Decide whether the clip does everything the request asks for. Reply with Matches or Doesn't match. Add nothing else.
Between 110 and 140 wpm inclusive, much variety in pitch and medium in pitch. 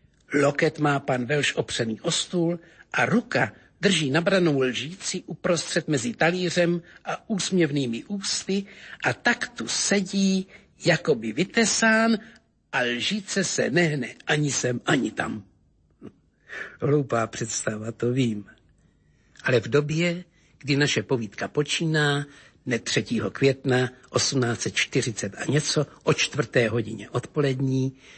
Matches